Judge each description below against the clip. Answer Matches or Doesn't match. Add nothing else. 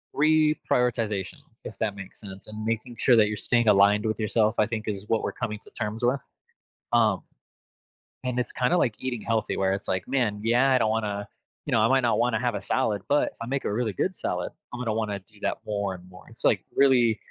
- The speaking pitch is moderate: Doesn't match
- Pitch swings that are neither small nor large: Matches